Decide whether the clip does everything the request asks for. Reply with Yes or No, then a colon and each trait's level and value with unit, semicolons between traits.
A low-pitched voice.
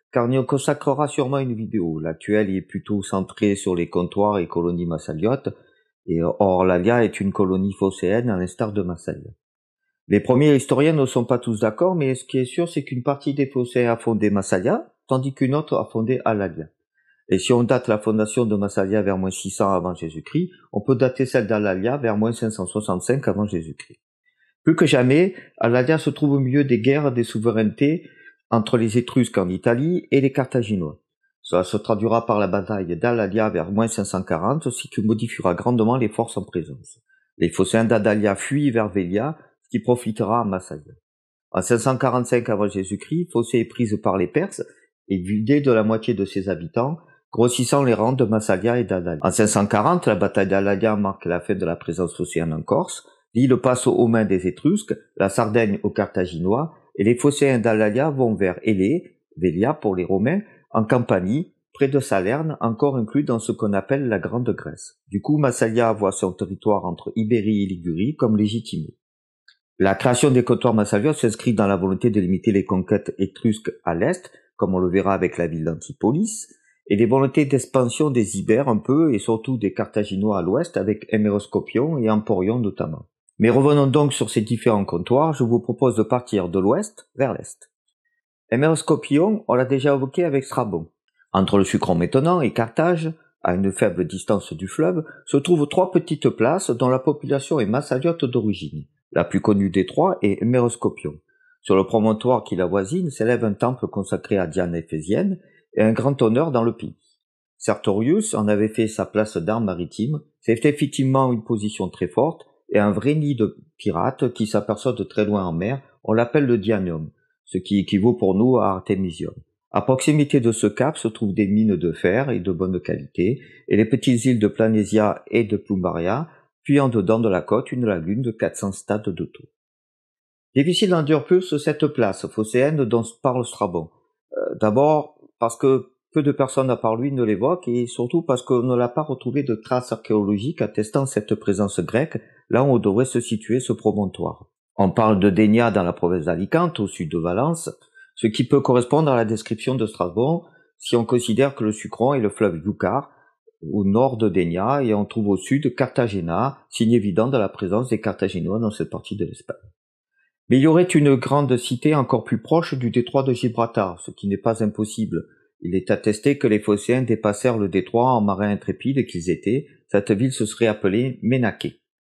Yes: low, 115 Hz